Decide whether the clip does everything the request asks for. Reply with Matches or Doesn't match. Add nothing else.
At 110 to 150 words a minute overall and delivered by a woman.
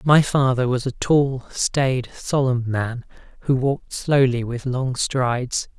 Doesn't match